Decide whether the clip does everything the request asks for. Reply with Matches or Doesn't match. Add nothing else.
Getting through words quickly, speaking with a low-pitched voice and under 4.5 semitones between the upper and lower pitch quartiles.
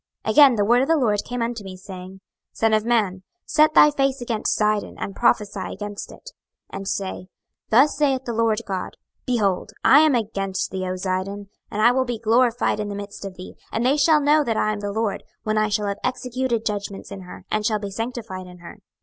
Doesn't match